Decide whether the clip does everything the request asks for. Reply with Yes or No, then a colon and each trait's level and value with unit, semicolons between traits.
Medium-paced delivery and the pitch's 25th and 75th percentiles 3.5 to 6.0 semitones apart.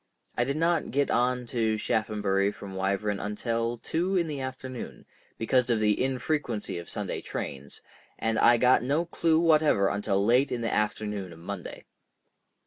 Yes: average, 160 wpm; average, 4.4 semitones